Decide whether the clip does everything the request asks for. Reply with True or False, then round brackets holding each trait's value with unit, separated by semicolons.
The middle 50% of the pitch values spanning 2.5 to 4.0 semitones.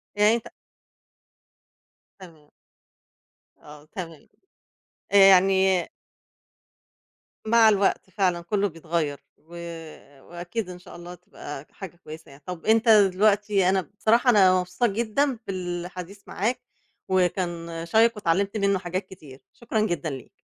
True (3.2 semitones)